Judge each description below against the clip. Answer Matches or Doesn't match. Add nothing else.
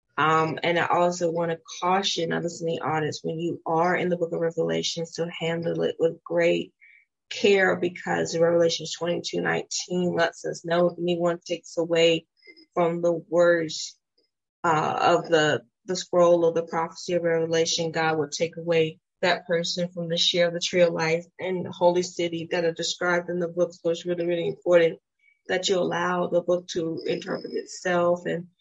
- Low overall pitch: Doesn't match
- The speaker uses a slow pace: Doesn't match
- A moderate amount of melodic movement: Doesn't match